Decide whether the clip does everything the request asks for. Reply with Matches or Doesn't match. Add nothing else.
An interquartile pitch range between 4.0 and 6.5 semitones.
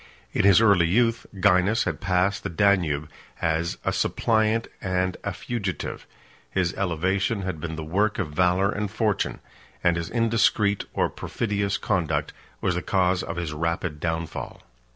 Doesn't match